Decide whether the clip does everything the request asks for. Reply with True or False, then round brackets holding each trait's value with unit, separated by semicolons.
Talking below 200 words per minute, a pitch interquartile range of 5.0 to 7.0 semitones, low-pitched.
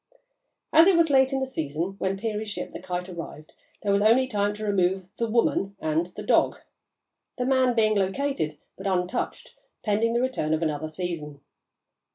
False (180 wpm; 5.3 semitones; 200 Hz)